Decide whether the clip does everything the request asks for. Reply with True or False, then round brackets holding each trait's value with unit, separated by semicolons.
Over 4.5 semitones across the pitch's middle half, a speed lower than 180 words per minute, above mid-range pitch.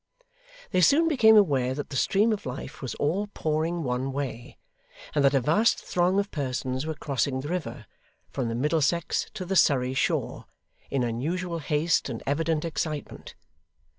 False (4.9 semitones; 165 wpm; 150 Hz)